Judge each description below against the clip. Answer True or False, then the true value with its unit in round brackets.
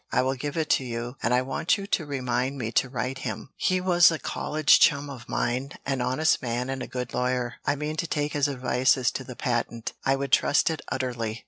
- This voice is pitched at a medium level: False (130 Hz)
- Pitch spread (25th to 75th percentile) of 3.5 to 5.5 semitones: False (2.7 semitones)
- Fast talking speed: True (235 wpm)